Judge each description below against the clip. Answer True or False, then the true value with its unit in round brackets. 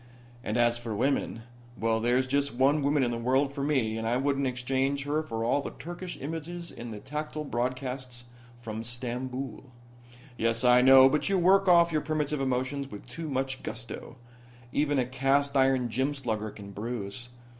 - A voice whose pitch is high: False (130 Hz)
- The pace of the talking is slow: False (175 wpm)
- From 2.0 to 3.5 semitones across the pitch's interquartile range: True (3.1 semitones)